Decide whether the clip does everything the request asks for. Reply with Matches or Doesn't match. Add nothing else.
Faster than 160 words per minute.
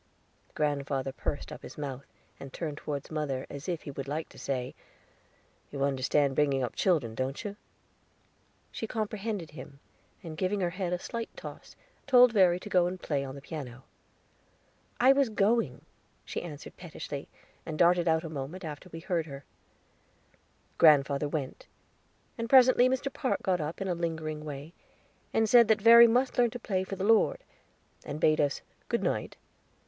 Matches